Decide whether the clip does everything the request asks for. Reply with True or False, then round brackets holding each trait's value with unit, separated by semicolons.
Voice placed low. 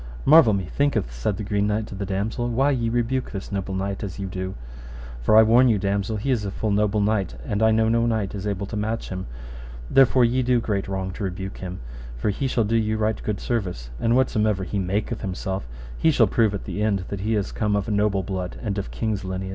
True (105 Hz)